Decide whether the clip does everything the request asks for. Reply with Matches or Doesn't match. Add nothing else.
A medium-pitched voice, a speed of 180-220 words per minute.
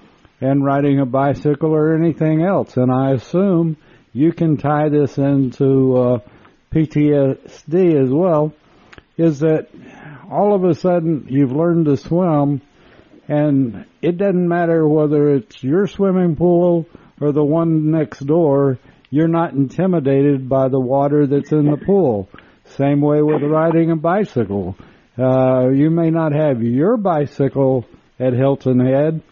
Doesn't match